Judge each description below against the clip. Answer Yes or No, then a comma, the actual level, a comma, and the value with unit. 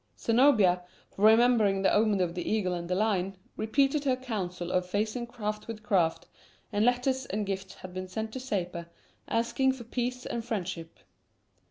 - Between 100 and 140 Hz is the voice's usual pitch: No, high, 215 Hz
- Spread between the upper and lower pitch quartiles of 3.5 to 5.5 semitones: Yes, average, 4.5 semitones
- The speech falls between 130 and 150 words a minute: No, average, 165 wpm